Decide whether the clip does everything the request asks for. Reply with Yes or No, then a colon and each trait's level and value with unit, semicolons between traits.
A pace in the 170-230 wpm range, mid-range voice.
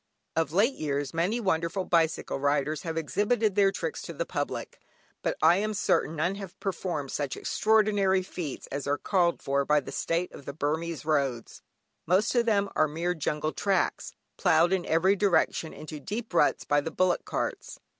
Yes: average, 175 wpm; medium, 170 Hz